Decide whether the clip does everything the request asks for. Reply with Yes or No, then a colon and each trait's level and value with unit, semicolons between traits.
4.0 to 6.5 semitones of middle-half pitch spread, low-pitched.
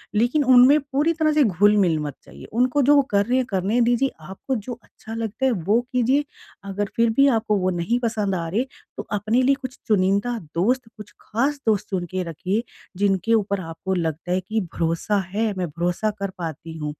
No: average, 4.9 semitones; high, 210 Hz